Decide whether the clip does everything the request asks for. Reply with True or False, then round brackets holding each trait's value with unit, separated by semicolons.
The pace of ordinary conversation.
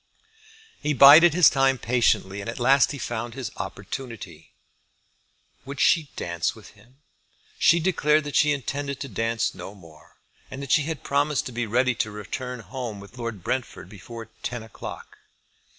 True (165 wpm)